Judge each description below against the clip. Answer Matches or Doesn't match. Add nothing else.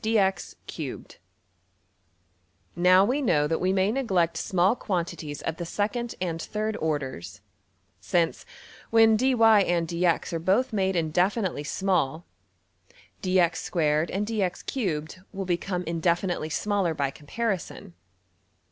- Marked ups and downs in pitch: Doesn't match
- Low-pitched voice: Doesn't match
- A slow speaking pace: Matches